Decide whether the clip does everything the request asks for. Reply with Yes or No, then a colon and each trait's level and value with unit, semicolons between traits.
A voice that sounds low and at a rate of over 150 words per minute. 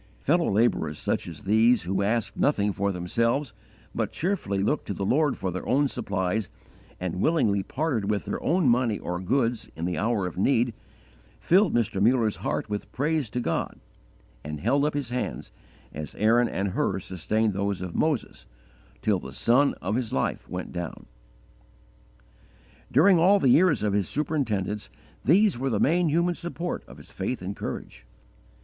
Yes: low, 115 Hz; average, 170 wpm